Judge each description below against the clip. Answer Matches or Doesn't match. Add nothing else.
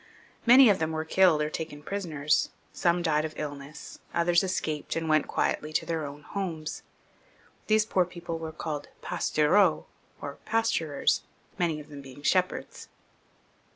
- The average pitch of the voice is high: Doesn't match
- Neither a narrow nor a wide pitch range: Matches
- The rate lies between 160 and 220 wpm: Doesn't match